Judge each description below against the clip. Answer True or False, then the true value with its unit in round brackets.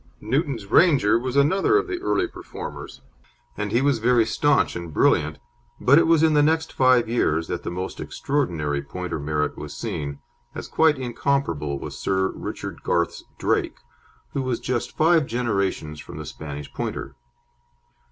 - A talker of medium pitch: False (120 Hz)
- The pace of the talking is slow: False (160 wpm)